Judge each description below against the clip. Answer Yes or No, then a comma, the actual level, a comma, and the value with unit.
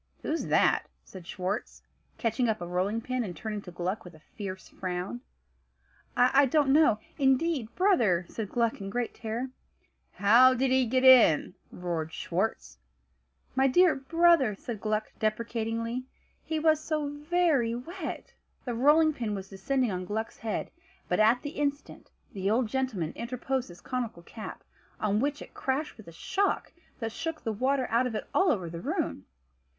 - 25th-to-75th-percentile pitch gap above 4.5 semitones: Yes, average, 5.2 semitones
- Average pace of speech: Yes, average, 165 wpm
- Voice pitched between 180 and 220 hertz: No, high, 235 Hz